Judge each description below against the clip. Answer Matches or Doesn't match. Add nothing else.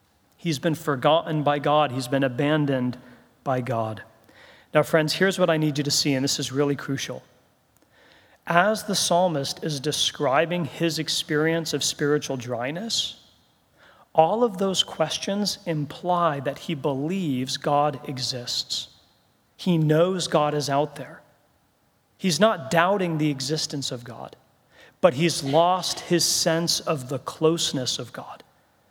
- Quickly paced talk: Doesn't match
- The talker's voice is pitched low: Doesn't match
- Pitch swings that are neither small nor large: Matches